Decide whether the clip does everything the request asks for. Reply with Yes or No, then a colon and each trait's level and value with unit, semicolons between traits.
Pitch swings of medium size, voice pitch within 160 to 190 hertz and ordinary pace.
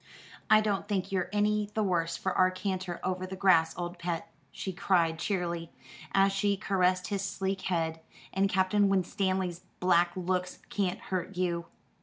No: narrow, 1.9 semitones; medium, 185 Hz; average, 160 wpm